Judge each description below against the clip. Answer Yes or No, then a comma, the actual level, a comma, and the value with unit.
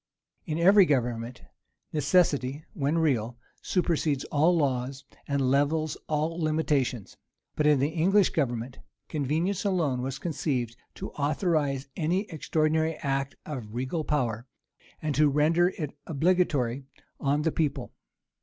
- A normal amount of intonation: Yes, average, 3.3 semitones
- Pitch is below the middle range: No, medium, 150 Hz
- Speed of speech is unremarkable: No, slow, 125 wpm